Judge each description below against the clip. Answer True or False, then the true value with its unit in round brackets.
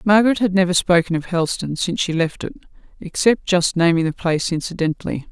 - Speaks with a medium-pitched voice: True (175 Hz)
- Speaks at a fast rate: False (180 wpm)